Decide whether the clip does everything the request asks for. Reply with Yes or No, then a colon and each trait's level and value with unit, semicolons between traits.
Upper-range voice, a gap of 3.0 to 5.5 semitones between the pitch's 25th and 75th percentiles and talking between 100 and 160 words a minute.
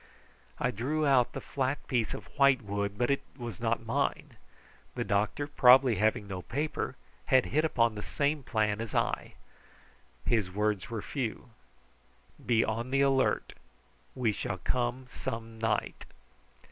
No: low, 120 Hz; average, 3.8 semitones; average, 145 wpm